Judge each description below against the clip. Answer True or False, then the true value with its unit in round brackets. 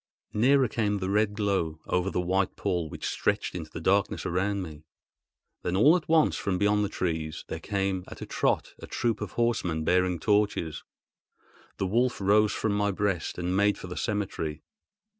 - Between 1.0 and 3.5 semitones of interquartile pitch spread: True (2.8 semitones)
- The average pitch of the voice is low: True (100 Hz)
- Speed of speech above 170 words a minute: True (180 wpm)